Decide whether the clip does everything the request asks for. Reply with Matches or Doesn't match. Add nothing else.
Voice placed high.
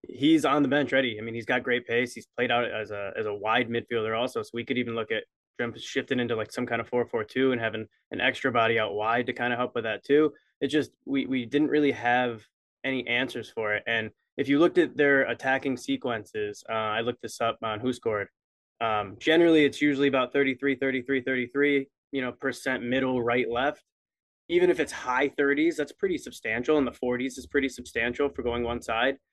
Doesn't match